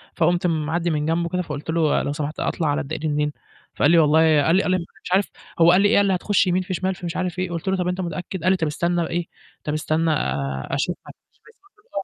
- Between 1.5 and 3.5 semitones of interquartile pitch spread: Yes, average, 3.0 semitones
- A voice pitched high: No, medium, 170 Hz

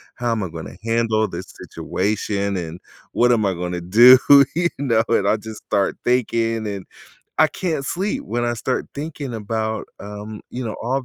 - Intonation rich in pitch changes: No, average, 3.2 semitones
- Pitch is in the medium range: No, low, 110 Hz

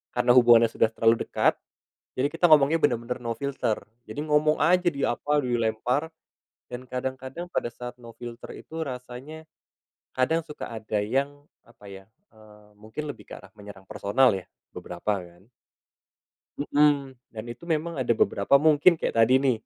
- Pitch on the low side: Yes, low, 125 Hz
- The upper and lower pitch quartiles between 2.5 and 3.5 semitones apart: No, average, 4.4 semitones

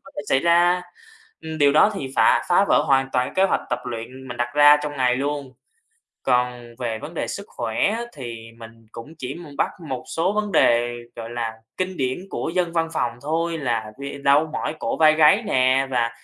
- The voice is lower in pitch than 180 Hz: Yes, medium, 140 Hz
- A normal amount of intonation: Yes, average, 5.0 semitones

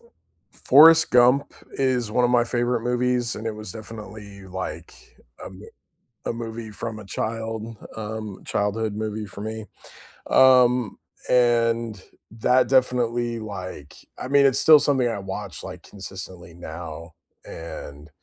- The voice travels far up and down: No, average, 3.5 semitones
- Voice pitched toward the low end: Yes, low, 110 Hz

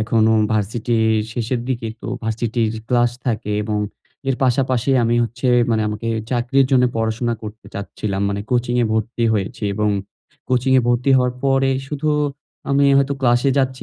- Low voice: Yes, low, 120 Hz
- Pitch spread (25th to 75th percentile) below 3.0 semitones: Yes, narrow, 2.6 semitones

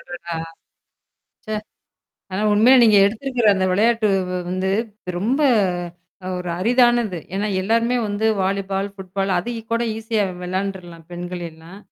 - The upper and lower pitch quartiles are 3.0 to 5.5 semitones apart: Yes, average, 3.8 semitones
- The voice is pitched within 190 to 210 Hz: Yes, high, 200 Hz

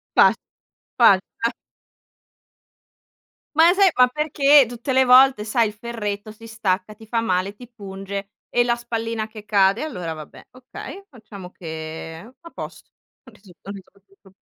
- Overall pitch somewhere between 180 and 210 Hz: No, high, 220 Hz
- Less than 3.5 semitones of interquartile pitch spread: No, average, 3.9 semitones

